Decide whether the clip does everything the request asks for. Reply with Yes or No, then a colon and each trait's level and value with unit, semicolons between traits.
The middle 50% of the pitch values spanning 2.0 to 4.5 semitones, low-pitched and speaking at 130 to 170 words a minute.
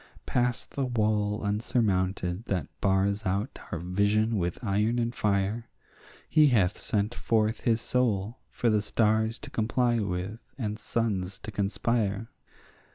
Yes: average, 2.8 semitones; low, 105 Hz; slow, 135 wpm